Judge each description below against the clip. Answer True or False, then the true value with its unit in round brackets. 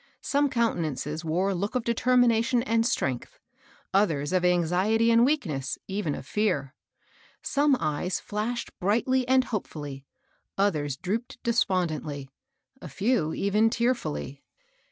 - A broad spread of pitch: True (7.1 semitones)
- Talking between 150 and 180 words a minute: False (135 wpm)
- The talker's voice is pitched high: True (200 Hz)